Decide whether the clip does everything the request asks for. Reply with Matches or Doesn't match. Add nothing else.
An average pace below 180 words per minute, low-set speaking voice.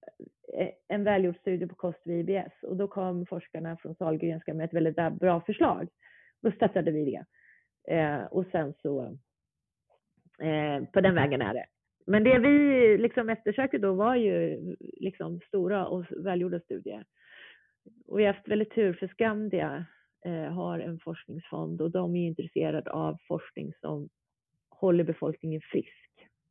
Doesn't match